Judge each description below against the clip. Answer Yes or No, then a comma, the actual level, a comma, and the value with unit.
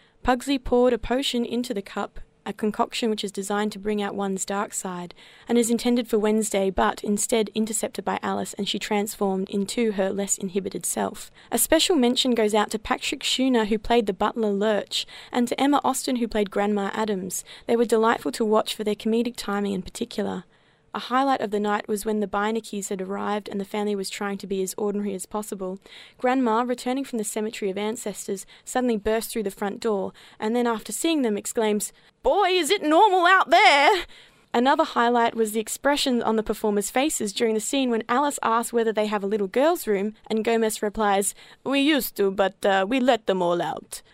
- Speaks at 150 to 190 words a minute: No, fast, 205 wpm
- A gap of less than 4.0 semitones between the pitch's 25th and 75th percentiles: Yes, average, 2.8 semitones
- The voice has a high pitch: Yes, high, 220 Hz